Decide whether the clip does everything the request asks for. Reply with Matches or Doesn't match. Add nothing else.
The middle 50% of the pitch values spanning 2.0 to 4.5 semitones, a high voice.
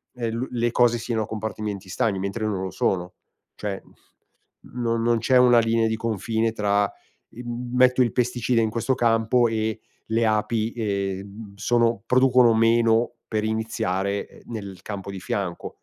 Doesn't match